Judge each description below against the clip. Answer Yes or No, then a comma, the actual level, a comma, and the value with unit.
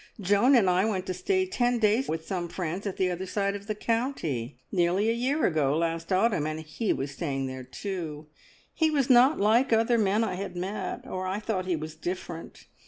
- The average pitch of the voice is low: No, high, 190 Hz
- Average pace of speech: No, fast, 210 wpm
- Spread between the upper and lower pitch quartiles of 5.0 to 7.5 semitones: Yes, average, 5.3 semitones